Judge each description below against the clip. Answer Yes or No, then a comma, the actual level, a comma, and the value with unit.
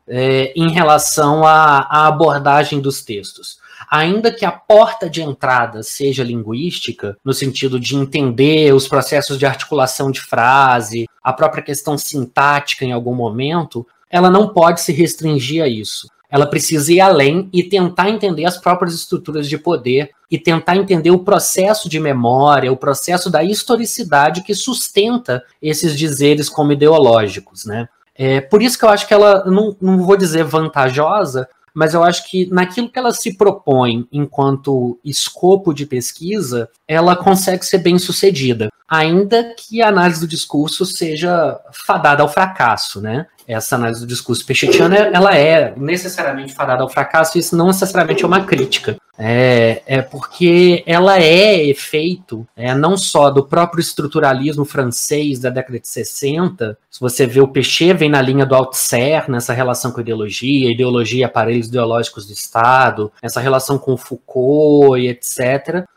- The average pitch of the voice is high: No, medium, 150 Hz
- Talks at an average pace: Yes, average, 160 wpm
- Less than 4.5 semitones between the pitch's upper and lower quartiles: No, average, 5.3 semitones